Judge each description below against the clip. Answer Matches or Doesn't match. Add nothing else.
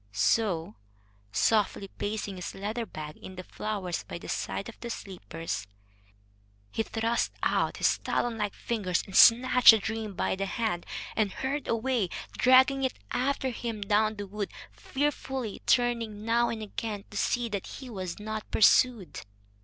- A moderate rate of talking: Matches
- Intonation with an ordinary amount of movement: Matches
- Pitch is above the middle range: Matches